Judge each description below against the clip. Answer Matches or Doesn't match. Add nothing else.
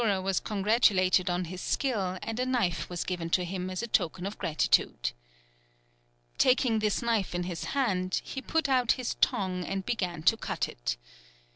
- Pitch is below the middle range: Doesn't match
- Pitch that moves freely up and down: Doesn't match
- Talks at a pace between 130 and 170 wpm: Doesn't match